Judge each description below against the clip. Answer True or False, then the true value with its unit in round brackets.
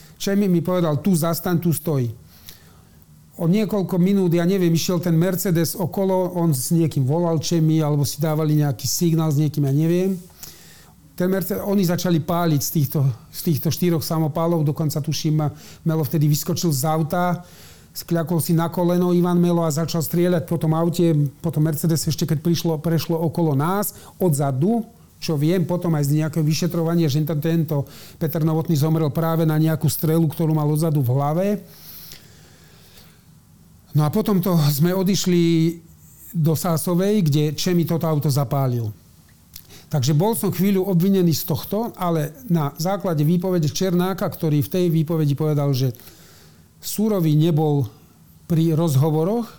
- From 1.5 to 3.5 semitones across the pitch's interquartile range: True (2.6 semitones)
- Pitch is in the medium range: True (165 Hz)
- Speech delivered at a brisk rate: False (150 wpm)